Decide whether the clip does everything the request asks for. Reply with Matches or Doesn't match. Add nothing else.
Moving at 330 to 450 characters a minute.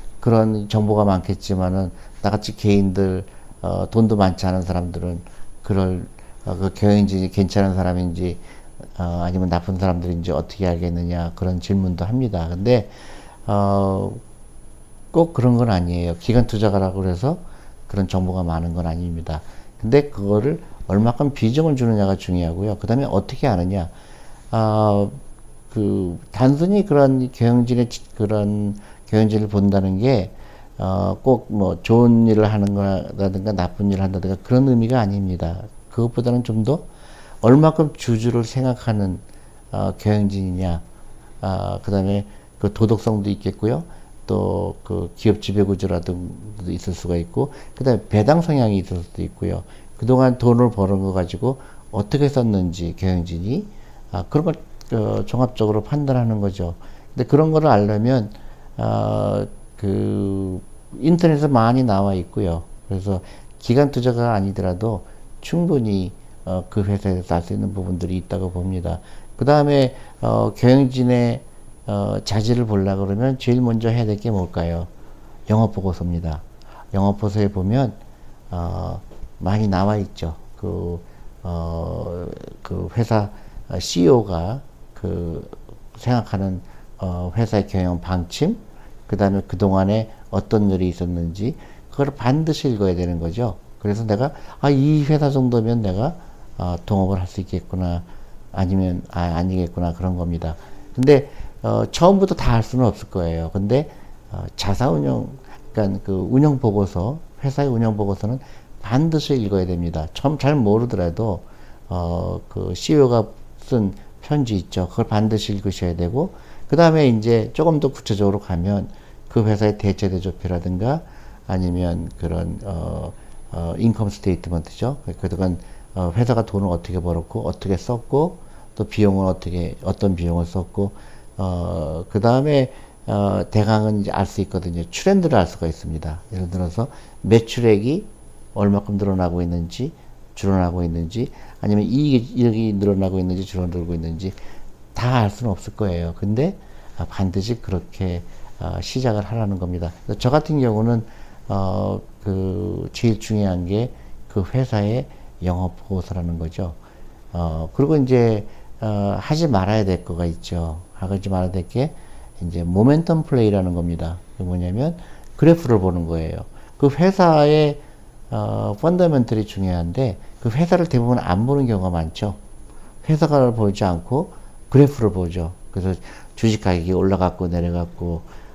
Doesn't match